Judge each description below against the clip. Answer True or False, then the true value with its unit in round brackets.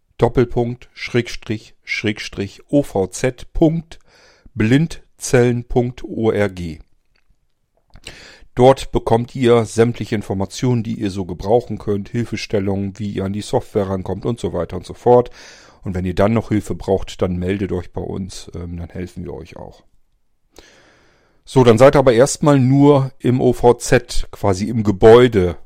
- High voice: False (110 Hz)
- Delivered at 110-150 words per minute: True (130 wpm)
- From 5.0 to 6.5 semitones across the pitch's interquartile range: False (4.0 semitones)